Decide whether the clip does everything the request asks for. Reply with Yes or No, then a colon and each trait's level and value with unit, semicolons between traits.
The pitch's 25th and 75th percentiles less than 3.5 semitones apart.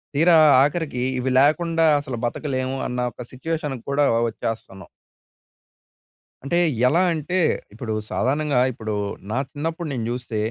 No: average, 4.6 semitones